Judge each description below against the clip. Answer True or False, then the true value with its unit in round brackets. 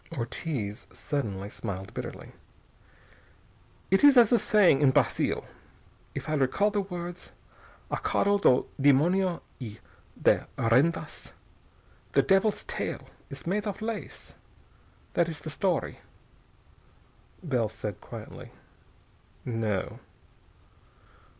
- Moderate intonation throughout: False (8.5 semitones)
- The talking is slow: True (105 wpm)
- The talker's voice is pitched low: False (155 Hz)